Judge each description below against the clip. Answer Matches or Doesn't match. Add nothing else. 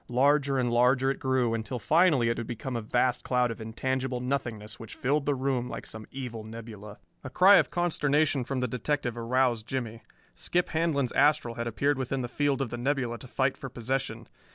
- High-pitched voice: Doesn't match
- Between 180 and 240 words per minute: Matches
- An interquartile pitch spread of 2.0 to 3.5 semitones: Matches